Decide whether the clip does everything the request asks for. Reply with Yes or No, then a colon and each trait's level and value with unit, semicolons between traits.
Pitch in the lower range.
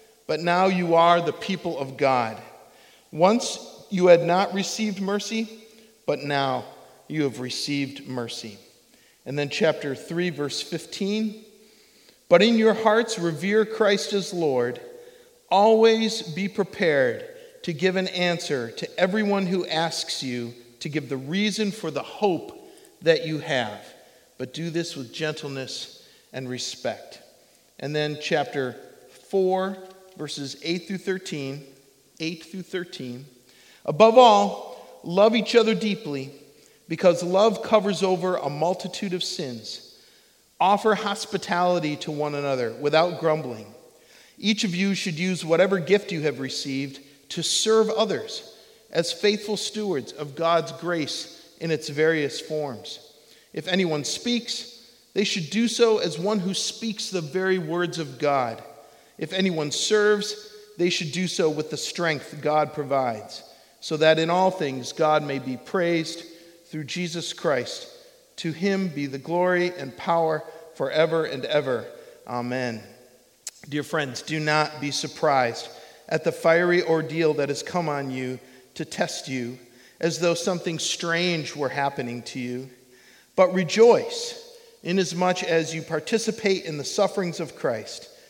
No: medium, 170 Hz